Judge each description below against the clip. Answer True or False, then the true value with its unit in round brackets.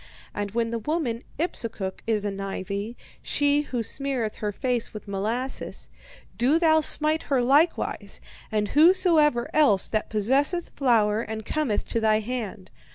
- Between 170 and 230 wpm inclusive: False (145 wpm)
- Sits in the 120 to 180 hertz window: False (235 Hz)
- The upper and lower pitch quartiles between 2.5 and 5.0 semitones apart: False (5.4 semitones)